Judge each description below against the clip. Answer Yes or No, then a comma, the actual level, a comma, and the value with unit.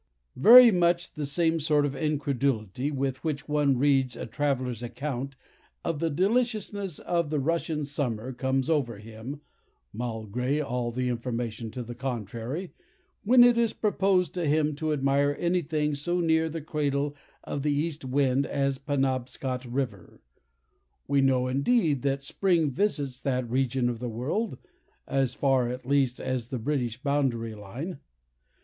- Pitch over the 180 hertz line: No, medium, 140 Hz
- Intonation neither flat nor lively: Yes, average, 3.6 semitones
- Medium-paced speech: Yes, average, 150 wpm